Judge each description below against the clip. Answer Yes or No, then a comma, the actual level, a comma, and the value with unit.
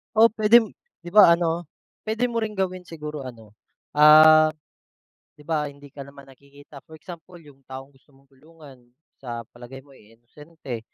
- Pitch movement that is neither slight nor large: Yes, average, 3.9 semitones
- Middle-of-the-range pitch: Yes, medium, 150 Hz